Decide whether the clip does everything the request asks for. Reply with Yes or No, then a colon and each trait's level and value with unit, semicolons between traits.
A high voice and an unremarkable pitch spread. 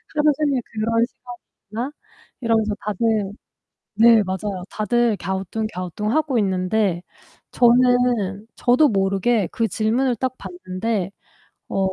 Yes: high, 220 Hz; average, 3.7 semitones